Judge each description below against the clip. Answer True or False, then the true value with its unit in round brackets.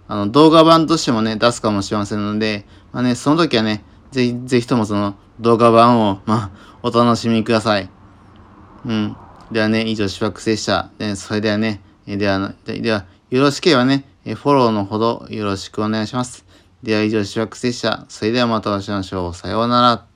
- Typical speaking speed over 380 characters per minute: False (360 characters per minute)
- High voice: False (110 Hz)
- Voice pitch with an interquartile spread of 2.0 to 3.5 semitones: True (2.7 semitones)